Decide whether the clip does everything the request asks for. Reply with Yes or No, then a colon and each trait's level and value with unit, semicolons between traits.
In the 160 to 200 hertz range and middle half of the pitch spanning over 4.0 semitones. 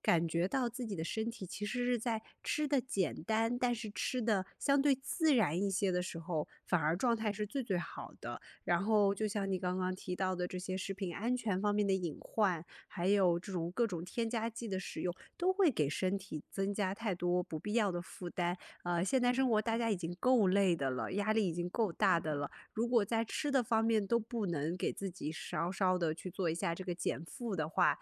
Yes: high, 195 Hz; average, 4.4 semitones